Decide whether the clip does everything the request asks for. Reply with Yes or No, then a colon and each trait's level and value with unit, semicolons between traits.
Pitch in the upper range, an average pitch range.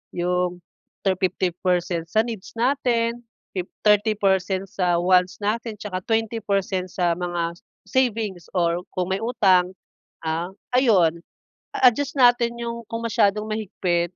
Yes: high, 195 Hz; average, 4.2 semitones